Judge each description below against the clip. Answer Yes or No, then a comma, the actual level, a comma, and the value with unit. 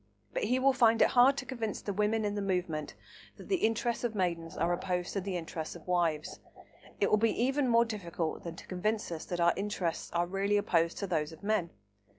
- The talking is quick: Yes, fast, 220 wpm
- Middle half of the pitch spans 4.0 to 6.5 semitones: Yes, average, 4.7 semitones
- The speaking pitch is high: Yes, high, 195 Hz